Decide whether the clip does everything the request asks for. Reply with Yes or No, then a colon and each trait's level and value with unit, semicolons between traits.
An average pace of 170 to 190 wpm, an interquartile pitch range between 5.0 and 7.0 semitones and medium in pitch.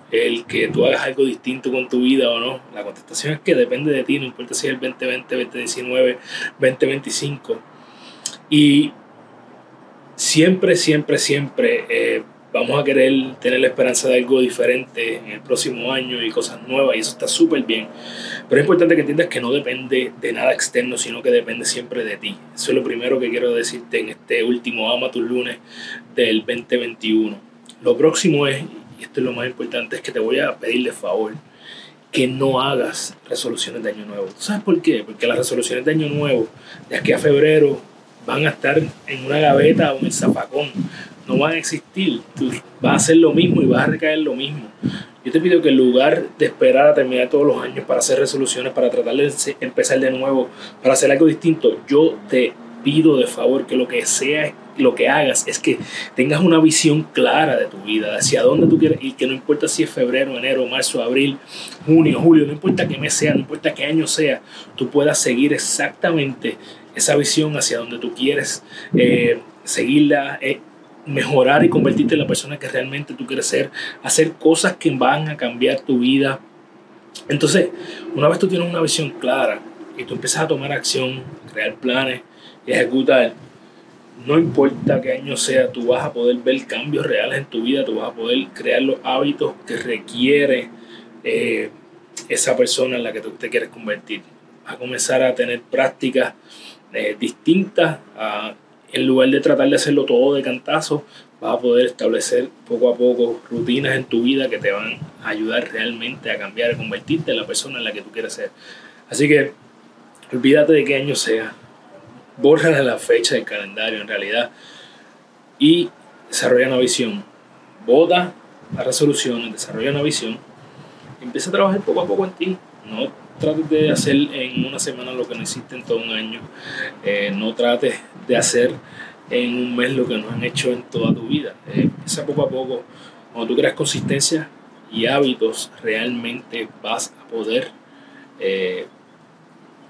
Yes: average, 185 wpm; wide, 5.6 semitones; medium, 145 Hz